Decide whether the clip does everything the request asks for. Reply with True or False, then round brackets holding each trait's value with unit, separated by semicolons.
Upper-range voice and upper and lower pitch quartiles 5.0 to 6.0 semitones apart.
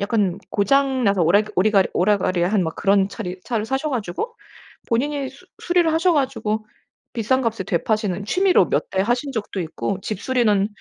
True (215 Hz; 5.3 semitones)